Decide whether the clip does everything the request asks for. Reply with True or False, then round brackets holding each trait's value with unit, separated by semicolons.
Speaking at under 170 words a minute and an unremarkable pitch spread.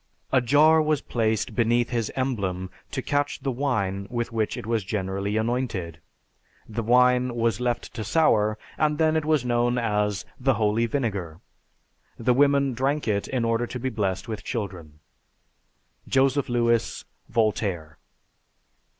True (145 wpm; 3.8 semitones)